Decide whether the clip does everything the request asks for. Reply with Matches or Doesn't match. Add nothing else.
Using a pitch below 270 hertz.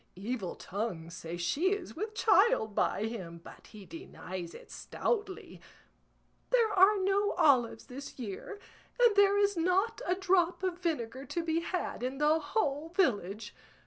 Doesn't match